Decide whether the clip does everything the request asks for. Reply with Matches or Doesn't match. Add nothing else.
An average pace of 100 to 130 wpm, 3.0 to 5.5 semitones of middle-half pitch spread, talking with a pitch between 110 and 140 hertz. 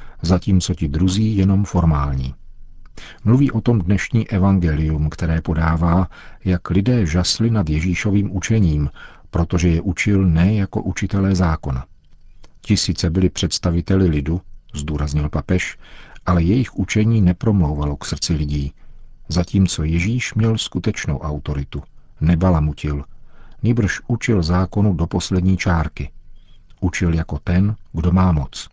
Doesn't match